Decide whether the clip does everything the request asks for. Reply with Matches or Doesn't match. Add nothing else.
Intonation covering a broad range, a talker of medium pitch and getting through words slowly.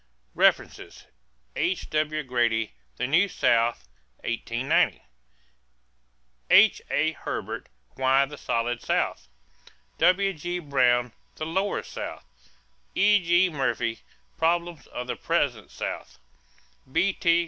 Matches